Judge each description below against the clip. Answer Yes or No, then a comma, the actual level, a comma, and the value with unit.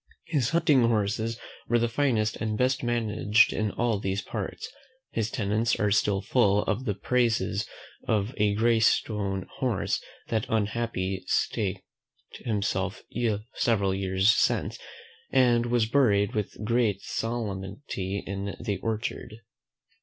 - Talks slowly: Yes, slow, 125 wpm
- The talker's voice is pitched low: Yes, low, 110 Hz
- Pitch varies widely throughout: No, average, 2.8 semitones